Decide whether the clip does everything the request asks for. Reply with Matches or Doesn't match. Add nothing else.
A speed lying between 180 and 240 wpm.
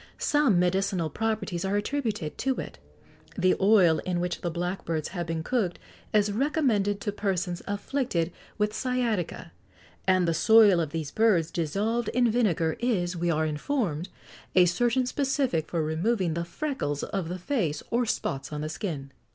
Doesn't match